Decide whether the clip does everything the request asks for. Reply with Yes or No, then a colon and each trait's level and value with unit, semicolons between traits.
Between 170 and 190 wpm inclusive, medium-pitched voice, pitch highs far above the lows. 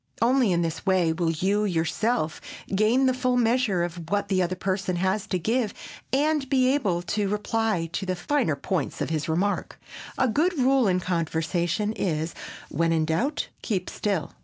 No: average, 175 wpm; high, 195 Hz; wide, 5.8 semitones